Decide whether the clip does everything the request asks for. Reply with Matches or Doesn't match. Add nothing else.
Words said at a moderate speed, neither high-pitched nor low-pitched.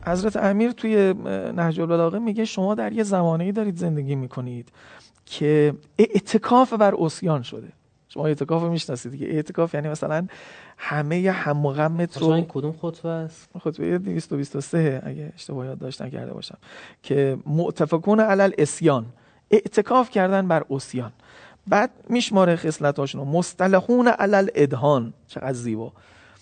Matches